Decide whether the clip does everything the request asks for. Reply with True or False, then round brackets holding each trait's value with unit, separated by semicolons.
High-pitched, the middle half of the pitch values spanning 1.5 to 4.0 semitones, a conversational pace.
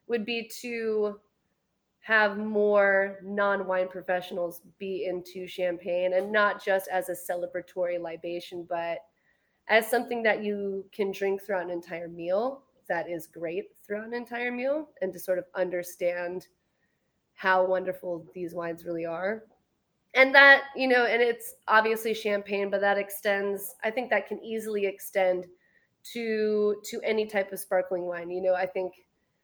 True (195 Hz; 3.3 semitones; 150 wpm)